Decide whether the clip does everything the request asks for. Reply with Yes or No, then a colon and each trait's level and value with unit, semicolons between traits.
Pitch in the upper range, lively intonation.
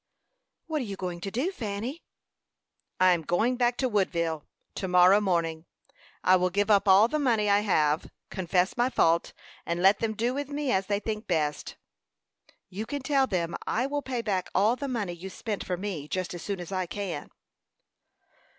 No: high, 200 Hz; average, 4.9 semitones